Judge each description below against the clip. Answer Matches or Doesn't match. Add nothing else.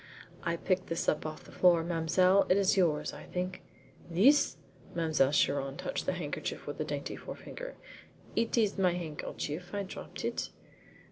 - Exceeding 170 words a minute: Doesn't match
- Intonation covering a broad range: Doesn't match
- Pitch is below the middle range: Doesn't match